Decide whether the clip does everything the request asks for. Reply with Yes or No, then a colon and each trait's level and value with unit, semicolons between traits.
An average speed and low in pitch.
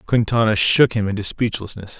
Yes: average, 150 wpm; low, 110 Hz